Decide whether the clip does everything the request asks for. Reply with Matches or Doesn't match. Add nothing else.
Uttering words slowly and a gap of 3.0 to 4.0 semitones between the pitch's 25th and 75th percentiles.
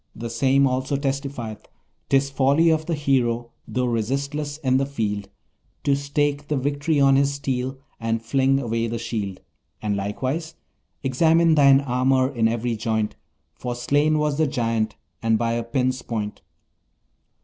Doesn't match